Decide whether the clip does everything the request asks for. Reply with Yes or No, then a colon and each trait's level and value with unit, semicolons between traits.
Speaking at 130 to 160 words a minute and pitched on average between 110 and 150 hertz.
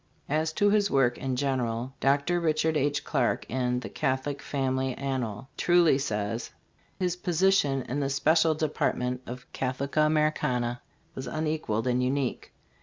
Yes: average, 155 wpm; low, 135 Hz